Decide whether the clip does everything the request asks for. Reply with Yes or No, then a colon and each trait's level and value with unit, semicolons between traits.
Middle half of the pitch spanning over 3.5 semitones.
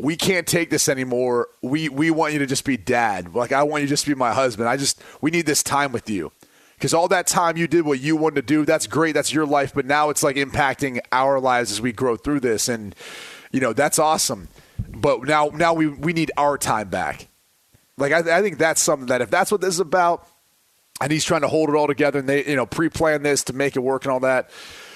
No: average, 3.1 semitones